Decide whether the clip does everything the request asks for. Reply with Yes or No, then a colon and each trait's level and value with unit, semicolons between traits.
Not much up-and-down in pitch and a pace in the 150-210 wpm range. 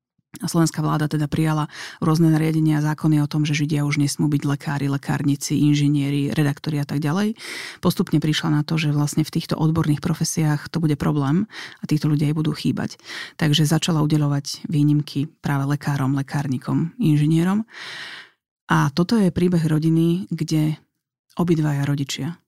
Yes: narrow, 1.8 semitones; average, 155 wpm